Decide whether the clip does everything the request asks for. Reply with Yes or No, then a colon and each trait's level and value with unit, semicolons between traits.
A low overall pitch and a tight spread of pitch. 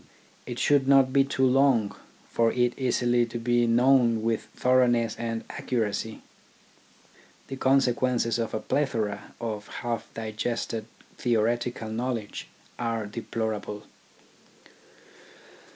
Yes: low, 120 Hz; narrow, 2.2 semitones